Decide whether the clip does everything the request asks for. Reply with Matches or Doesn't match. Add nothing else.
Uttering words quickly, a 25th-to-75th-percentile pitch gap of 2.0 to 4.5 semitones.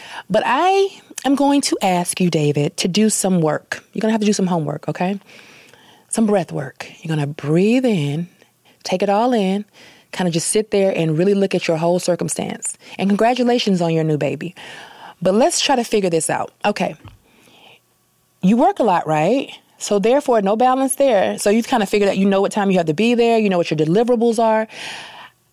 Doesn't match